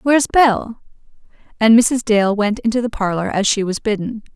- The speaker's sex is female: Yes, female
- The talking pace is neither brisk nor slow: Yes, average, 180 wpm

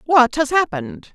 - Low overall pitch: No, high, 245 Hz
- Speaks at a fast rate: No, average, 155 wpm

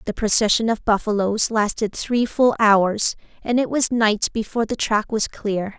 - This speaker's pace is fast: No, average, 175 wpm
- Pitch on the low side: No, high, 220 Hz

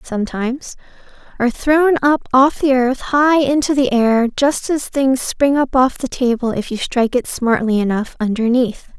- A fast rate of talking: No, average, 165 wpm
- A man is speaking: No, female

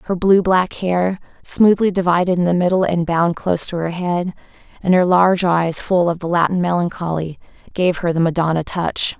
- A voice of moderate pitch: Yes, medium, 175 Hz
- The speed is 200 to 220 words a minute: No, average, 190 wpm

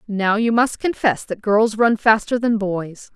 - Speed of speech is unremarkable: Yes, average, 190 wpm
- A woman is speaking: Yes, female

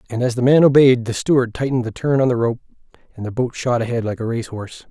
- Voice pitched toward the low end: Yes, low, 120 Hz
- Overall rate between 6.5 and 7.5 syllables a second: Yes, 6.8 syllables/s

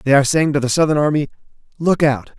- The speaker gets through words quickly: Yes, fast, 225 wpm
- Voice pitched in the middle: Yes, medium, 145 Hz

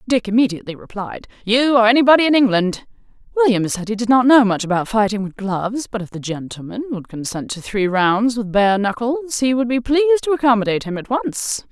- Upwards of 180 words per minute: Yes, fast, 205 wpm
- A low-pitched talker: No, high, 225 Hz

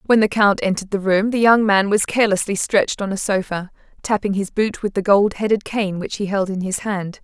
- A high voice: Yes, high, 200 Hz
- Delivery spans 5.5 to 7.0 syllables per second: Yes, 5.6 syllables/s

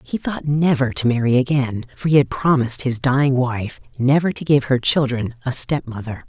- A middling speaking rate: Yes, average, 190 wpm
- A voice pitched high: No, low, 130 Hz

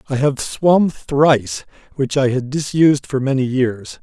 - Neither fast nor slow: Yes, average, 165 wpm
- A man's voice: Yes, male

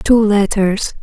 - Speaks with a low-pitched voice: No, high, 205 Hz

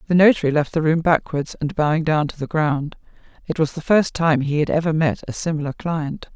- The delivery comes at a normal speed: No, fast, 225 wpm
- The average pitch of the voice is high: No, medium, 155 Hz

